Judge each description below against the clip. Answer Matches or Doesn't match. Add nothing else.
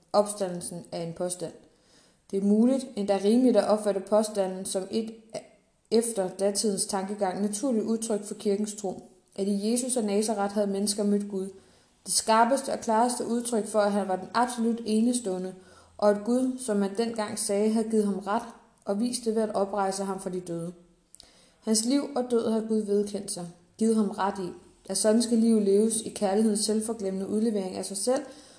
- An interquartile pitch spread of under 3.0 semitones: Matches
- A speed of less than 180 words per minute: Doesn't match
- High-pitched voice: Matches